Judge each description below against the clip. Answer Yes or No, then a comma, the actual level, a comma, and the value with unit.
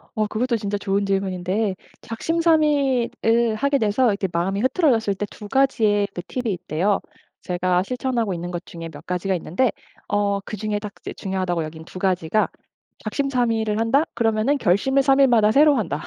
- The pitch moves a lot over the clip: No, average, 4.9 semitones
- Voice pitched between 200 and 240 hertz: Yes, high, 215 Hz